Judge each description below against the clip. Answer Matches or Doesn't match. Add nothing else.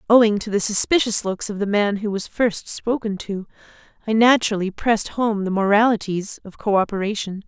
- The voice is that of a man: Doesn't match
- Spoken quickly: Doesn't match